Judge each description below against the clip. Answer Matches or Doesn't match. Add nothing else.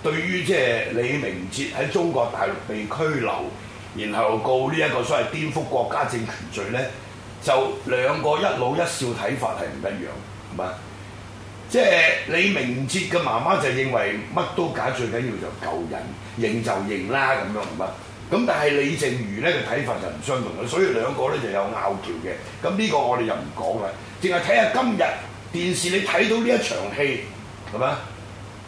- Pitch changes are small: Doesn't match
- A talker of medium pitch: Doesn't match